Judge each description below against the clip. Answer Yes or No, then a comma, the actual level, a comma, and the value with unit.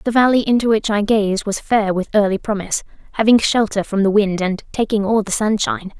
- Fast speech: Yes, fast, 210 wpm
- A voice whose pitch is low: No, high, 210 Hz